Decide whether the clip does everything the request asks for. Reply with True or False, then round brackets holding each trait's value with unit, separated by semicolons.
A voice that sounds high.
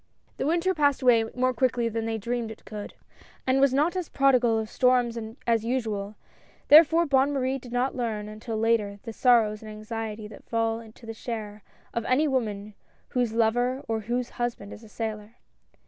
True (230 Hz)